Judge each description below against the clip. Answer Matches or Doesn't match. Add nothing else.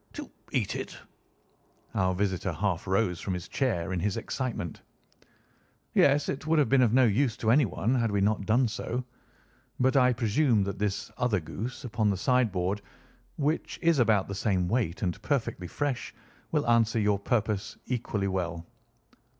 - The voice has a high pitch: Doesn't match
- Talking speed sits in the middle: Matches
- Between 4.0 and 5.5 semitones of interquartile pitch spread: Matches